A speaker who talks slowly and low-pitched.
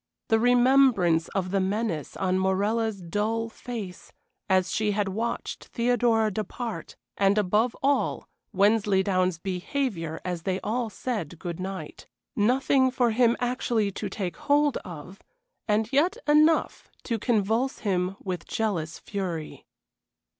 No: slow, 125 wpm; high, 210 Hz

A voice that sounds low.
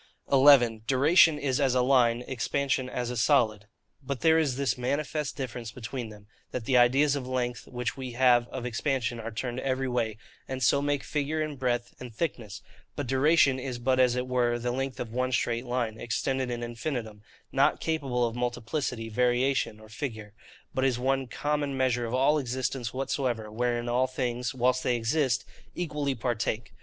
Yes: low, 125 Hz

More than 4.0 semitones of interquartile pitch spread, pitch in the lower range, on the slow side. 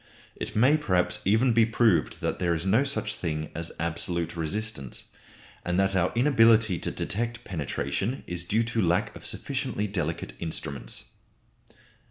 No: average, 5.2 semitones; very low, 95 Hz; average, 150 wpm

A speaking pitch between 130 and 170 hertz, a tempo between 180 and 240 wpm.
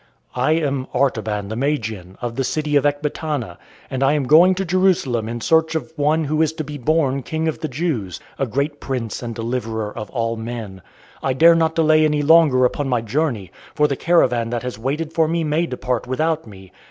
Yes: medium, 140 Hz; fast, 205 wpm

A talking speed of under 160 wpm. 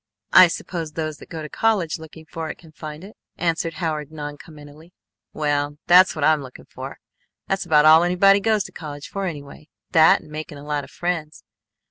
No: average, 190 wpm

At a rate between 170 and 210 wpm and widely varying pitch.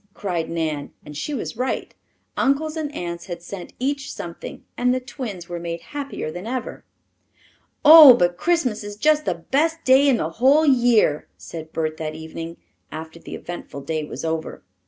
Yes: average, 175 wpm; wide, 8.8 semitones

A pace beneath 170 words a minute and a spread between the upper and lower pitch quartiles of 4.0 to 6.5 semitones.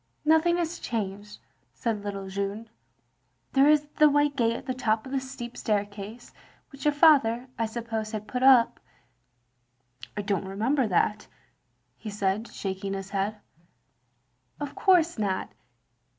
Yes: average, 150 wpm; average, 5.2 semitones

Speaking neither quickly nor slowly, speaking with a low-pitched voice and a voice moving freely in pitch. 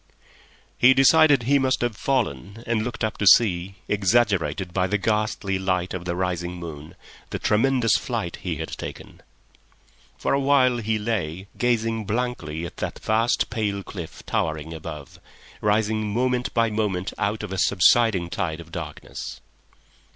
No: average, 150 wpm; low, 105 Hz; average, 4.7 semitones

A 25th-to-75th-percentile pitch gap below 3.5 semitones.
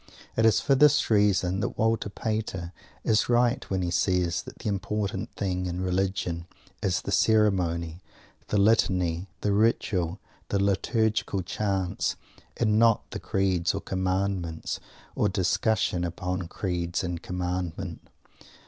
Yes: average, 3.0 semitones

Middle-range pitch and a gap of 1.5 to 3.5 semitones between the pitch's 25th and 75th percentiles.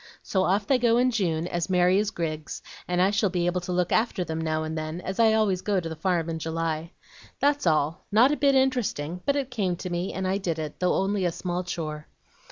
No: medium, 180 Hz; average, 4.1 semitones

